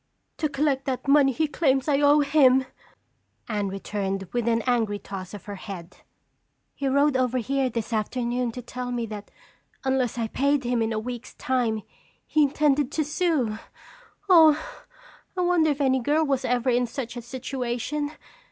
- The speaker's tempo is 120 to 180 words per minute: Yes, average, 170 wpm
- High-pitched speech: Yes, very high, 255 Hz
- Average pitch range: Yes, average, 3.7 semitones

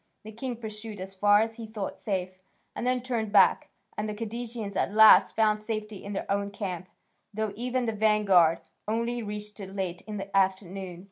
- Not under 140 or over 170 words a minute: No, average, 190 wpm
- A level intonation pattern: Yes, narrow, 2.2 semitones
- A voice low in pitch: No, high, 210 Hz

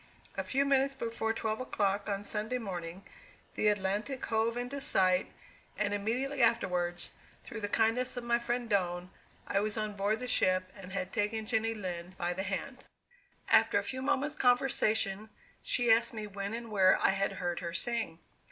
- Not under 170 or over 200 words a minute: Yes, average, 175 wpm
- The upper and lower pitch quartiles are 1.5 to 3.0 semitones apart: No, average, 3.7 semitones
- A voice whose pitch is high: Yes, high, 215 Hz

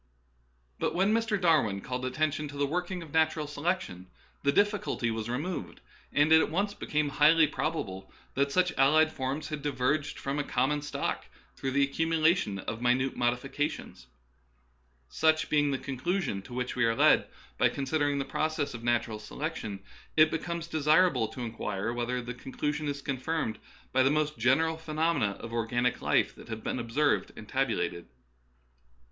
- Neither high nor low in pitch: Yes, medium, 145 Hz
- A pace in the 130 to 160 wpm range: No, average, 170 wpm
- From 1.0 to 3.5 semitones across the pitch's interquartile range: No, average, 4.4 semitones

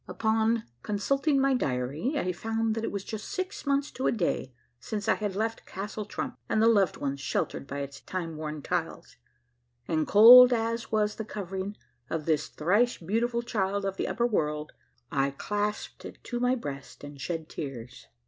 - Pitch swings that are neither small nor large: No, wide, 6.7 semitones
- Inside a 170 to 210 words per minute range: Yes, average, 180 wpm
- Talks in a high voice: Yes, high, 205 Hz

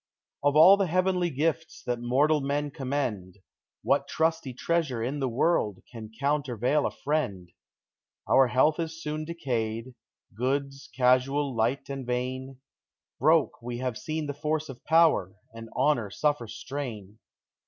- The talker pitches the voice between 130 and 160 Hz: Yes, low, 135 Hz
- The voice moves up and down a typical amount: Yes, average, 4.0 semitones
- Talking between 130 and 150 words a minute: Yes, average, 145 wpm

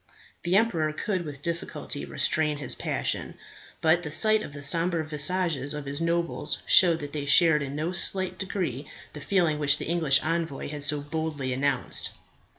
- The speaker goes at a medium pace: Yes, average, 170 wpm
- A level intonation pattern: No, average, 3.1 semitones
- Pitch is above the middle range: No, medium, 155 Hz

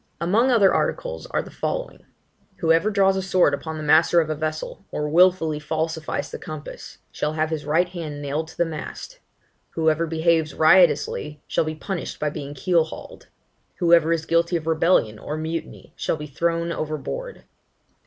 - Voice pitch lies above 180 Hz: No, medium, 160 Hz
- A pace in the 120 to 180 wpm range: Yes, average, 170 wpm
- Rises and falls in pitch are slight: Yes, narrow, 2.0 semitones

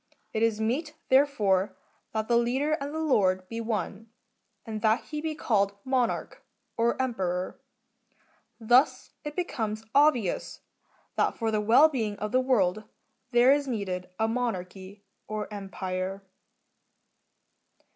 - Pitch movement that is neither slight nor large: Yes, average, 4.5 semitones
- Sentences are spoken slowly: Yes, slow, 125 wpm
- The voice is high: Yes, high, 225 Hz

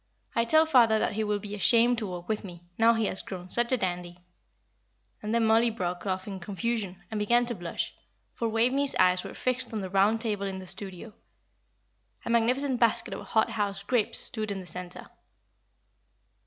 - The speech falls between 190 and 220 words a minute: Yes, average, 195 wpm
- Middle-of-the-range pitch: No, high, 215 Hz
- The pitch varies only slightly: No, average, 3.6 semitones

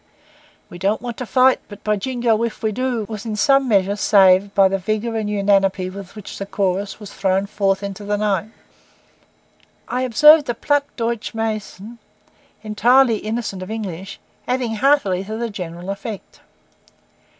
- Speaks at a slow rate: No, average, 160 wpm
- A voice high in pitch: Yes, high, 210 Hz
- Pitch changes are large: No, average, 3.1 semitones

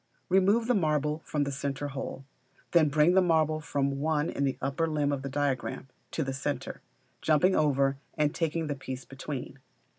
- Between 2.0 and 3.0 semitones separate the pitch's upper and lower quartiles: Yes, narrow, 2.5 semitones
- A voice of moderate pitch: Yes, medium, 145 Hz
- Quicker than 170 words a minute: Yes, average, 180 wpm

